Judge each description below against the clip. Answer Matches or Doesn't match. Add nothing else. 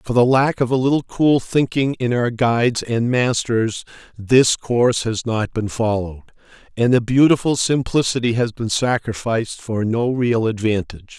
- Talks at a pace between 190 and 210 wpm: Doesn't match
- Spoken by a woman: Doesn't match